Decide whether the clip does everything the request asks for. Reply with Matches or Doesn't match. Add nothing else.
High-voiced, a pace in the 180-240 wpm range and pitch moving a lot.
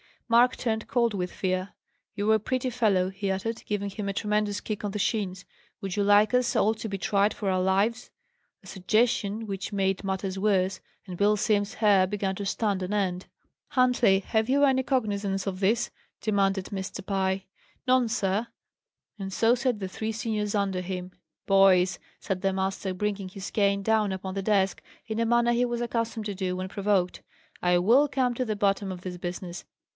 Doesn't match